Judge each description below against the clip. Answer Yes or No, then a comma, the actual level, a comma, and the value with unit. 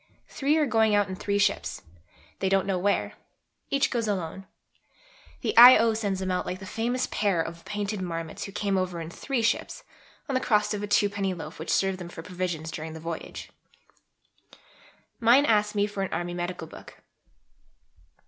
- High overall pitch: Yes, high, 195 Hz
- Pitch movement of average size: Yes, average, 3.2 semitones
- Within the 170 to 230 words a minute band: Yes, average, 180 wpm